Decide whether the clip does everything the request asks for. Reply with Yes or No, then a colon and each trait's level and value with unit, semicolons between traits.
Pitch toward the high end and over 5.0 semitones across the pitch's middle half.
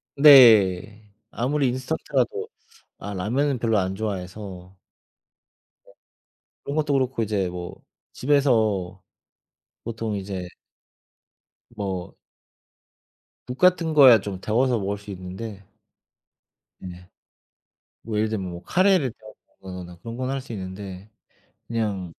No: low, 105 Hz; wide, 5.4 semitones